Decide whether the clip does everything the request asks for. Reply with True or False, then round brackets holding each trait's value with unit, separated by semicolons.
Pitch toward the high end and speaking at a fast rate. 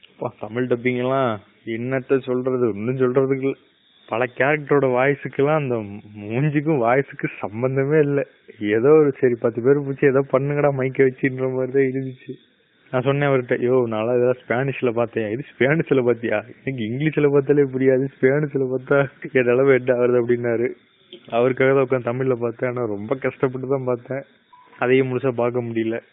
False (130 Hz; 135 wpm)